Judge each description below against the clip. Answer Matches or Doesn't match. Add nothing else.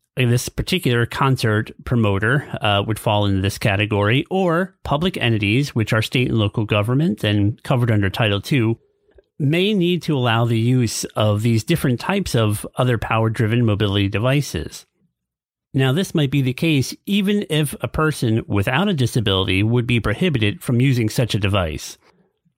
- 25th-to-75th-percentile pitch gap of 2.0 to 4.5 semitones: Doesn't match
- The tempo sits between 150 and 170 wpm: Matches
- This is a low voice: Matches